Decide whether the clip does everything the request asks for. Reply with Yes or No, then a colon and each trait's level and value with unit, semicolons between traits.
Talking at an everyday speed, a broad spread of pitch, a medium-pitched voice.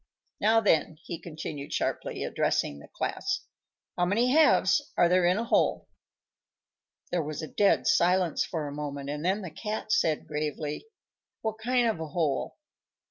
Yes: average, 160 wpm; wide, 6.1 semitones; medium, 175 Hz